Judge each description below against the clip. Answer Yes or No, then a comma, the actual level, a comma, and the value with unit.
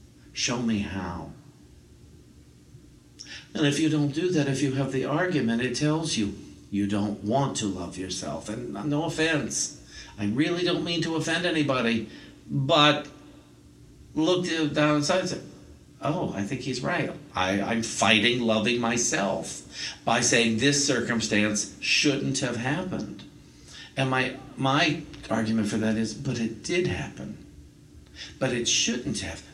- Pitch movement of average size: No, wide, 6.3 semitones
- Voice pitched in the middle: No, low, 125 Hz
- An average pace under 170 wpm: Yes, average, 145 wpm